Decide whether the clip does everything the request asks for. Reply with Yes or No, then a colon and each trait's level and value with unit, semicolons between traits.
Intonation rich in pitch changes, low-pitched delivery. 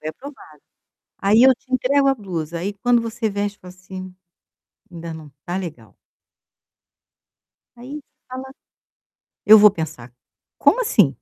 No: wide, 6.8 semitones; high, 200 Hz